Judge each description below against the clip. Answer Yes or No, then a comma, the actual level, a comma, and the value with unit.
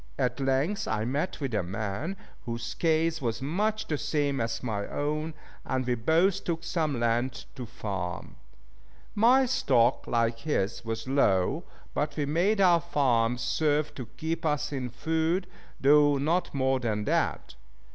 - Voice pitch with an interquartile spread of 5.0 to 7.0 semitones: Yes, wide, 5.4 semitones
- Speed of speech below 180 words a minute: Yes, average, 155 wpm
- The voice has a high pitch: No, medium, 140 Hz